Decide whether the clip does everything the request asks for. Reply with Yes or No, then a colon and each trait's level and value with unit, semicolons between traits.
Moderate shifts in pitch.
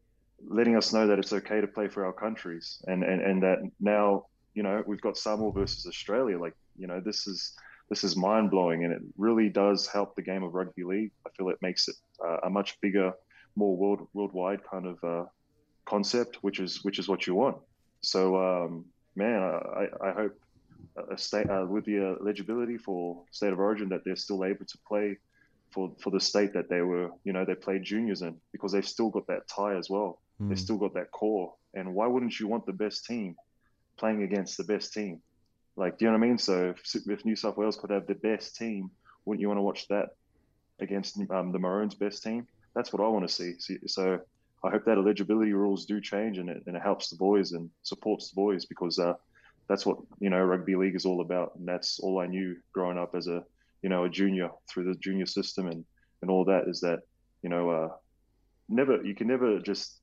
No: narrow, 2.1 semitones